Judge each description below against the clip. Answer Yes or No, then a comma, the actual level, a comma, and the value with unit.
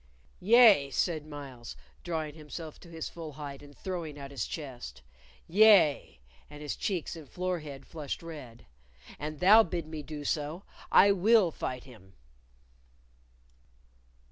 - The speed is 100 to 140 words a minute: Yes, slow, 135 wpm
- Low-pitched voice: No, medium, 155 Hz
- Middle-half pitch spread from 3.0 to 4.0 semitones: Yes, average, 3.6 semitones